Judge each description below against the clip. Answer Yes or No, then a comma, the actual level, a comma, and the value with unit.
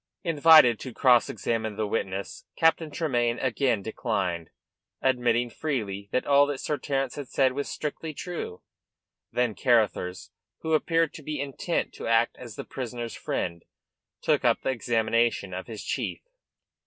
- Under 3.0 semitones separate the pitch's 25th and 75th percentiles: No, average, 4.4 semitones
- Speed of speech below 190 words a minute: Yes, average, 150 wpm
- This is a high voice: No, low, 125 Hz